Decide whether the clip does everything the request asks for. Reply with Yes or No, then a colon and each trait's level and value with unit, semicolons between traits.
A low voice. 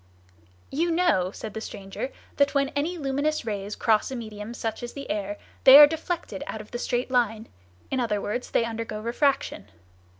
No: high, 240 Hz